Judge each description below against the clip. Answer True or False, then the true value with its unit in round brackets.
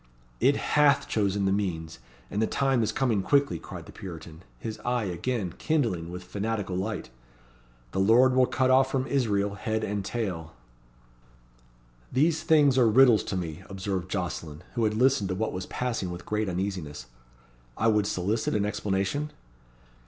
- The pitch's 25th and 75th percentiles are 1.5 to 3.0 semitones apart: False (5.3 semitones)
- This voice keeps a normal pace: True (160 wpm)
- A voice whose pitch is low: True (105 Hz)